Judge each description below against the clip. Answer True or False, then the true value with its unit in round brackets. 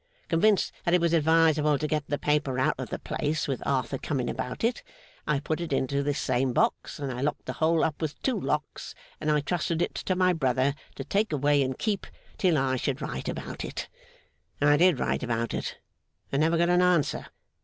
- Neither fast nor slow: False (210 wpm)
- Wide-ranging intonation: False (3.7 semitones)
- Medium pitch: True (150 Hz)